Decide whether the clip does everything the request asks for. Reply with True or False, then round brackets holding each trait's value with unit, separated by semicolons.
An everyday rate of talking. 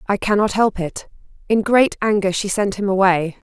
True (190 wpm)